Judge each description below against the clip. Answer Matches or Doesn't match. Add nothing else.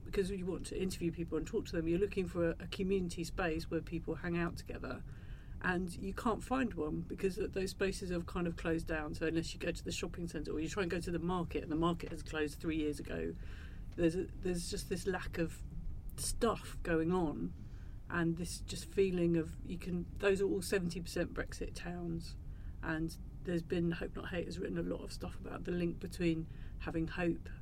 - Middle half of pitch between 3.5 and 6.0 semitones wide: Doesn't match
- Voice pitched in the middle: Matches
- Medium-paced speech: Doesn't match